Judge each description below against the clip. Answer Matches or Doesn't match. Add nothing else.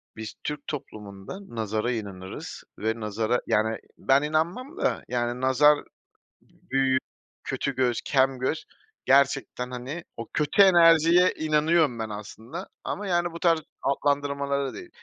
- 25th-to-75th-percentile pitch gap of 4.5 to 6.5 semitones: Matches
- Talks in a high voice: Doesn't match